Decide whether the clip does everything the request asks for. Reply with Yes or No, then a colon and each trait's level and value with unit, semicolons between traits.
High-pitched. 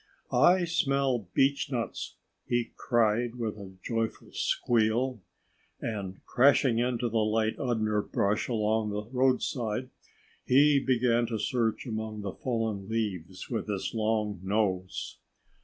No: low, 115 Hz